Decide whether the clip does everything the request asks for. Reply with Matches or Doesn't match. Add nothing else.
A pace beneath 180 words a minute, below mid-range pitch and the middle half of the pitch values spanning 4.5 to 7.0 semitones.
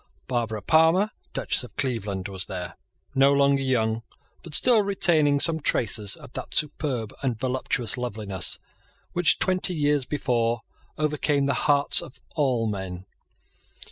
Matches